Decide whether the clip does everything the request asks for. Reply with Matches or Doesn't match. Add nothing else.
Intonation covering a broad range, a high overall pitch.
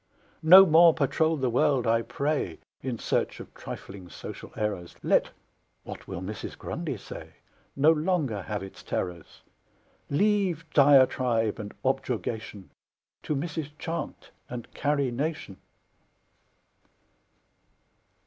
Doesn't match